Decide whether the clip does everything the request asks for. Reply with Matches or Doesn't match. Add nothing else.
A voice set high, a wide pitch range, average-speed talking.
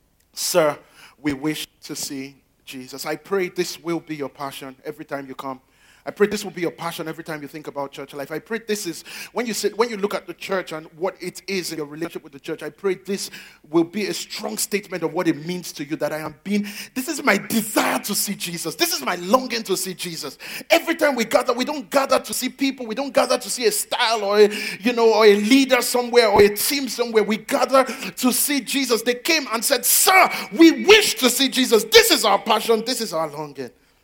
Doesn't match